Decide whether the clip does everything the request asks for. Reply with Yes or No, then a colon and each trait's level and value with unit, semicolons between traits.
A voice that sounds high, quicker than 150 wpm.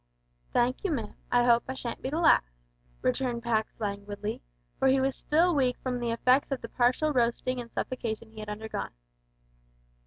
Yes: high, 240 Hz; average, 180 wpm